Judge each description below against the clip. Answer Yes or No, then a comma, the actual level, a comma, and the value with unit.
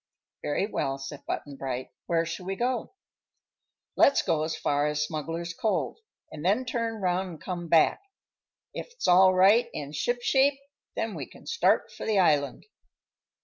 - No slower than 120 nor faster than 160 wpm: Yes, average, 155 wpm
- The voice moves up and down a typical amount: No, wide, 6.6 semitones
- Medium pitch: Yes, medium, 175 Hz